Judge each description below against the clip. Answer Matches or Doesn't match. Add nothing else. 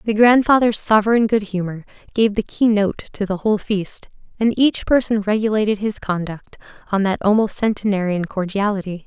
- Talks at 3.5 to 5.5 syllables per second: Matches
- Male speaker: Doesn't match